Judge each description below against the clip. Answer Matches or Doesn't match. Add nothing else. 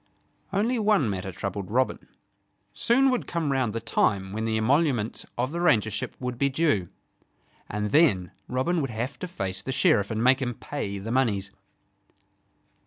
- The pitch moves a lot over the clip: Matches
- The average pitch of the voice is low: Matches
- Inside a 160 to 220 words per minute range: Matches